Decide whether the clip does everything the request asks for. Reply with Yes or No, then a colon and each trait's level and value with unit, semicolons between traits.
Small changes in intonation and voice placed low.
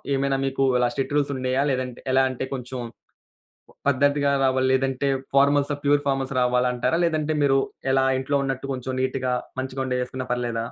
Yes: narrow, 1.5 semitones; low, 130 Hz